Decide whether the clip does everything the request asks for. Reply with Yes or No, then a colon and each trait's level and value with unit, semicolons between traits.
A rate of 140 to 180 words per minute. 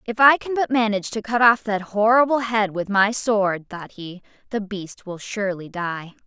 No: average, 200 wpm